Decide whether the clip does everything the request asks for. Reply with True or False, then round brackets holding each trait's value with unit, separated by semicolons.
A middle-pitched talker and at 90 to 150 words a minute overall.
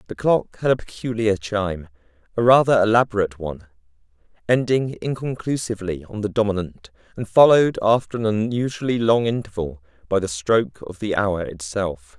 False (105 Hz; 145 wpm)